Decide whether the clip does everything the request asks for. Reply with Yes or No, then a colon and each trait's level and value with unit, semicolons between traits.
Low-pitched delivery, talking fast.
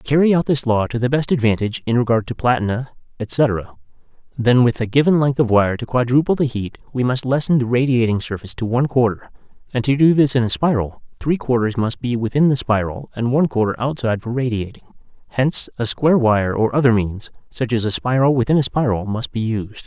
Yes: low, 120 Hz; fast, 215 wpm